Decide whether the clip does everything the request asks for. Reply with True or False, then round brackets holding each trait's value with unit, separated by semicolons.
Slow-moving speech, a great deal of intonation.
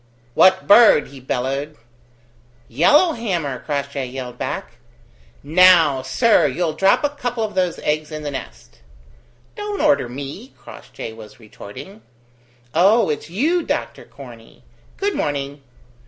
True (125 wpm; 8.0 semitones)